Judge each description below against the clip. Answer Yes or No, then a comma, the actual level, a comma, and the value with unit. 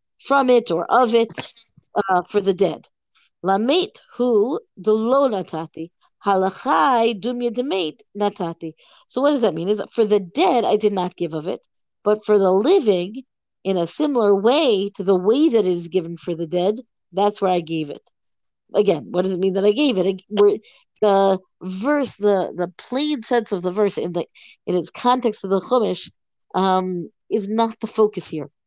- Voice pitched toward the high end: Yes, high, 205 Hz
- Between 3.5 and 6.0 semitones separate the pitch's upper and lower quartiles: Yes, average, 4.5 semitones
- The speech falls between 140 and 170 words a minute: No, average, 180 wpm